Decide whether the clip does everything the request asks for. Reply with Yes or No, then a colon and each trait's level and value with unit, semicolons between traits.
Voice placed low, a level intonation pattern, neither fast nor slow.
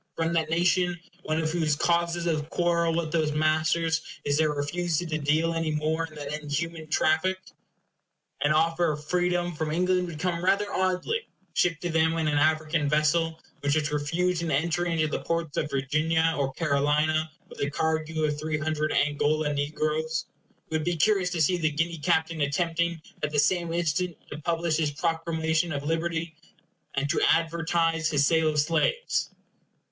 No: medium, 160 Hz; narrow, 1.9 semitones; average, 175 wpm